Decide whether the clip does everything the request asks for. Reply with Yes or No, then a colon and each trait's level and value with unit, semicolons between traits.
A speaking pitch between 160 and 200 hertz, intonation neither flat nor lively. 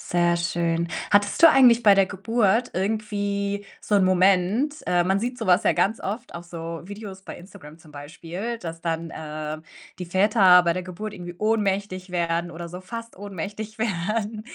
Yes: high, 190 Hz; average, 3.6 semitones